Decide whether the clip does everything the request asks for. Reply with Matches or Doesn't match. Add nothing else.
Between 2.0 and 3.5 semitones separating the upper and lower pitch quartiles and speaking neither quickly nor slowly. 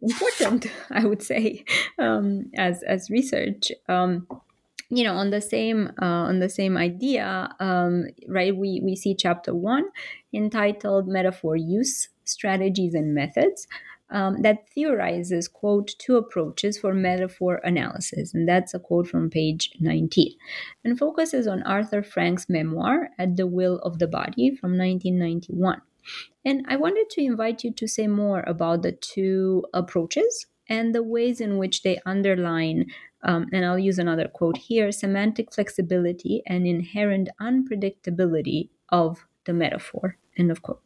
Doesn't match